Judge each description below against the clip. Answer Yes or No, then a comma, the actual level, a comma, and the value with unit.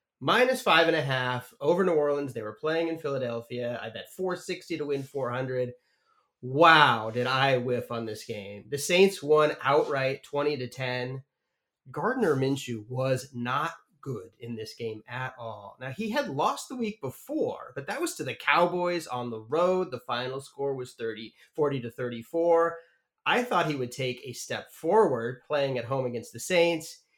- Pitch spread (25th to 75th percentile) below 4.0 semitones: No, average, 5.3 semitones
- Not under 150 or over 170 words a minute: No, average, 180 wpm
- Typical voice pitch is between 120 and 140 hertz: Yes, low, 135 Hz